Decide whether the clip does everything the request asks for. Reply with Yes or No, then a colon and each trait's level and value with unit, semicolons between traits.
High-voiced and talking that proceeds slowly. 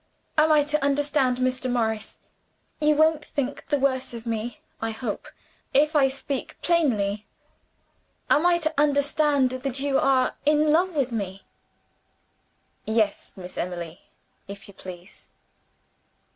Yes: very high, 270 Hz; slow, 130 wpm